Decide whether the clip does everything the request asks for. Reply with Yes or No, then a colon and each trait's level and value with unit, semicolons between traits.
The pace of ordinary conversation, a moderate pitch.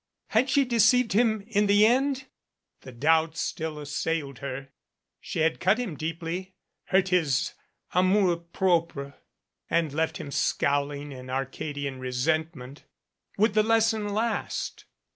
No: slow, 130 wpm; medium, 165 Hz